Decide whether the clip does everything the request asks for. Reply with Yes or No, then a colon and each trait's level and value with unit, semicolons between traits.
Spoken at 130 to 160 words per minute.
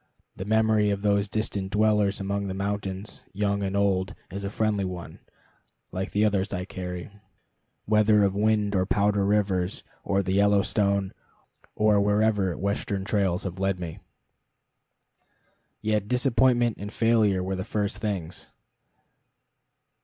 Yes: slow, 135 wpm